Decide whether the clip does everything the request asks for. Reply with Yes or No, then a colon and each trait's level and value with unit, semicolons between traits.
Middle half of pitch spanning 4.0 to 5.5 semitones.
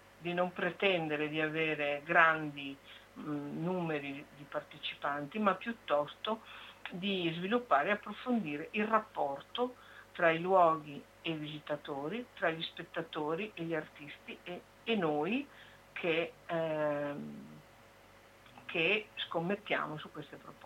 Yes: average, 4.3 semitones